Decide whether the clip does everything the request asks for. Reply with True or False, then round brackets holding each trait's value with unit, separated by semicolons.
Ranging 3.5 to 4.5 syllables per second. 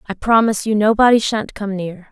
False (5.6 syllables/s)